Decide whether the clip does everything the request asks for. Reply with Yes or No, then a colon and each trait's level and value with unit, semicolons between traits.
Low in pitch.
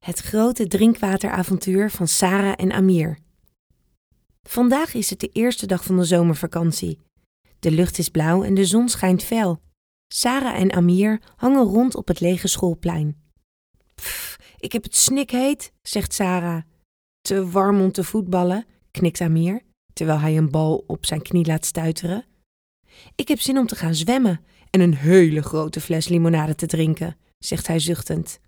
No: medium, 180 Hz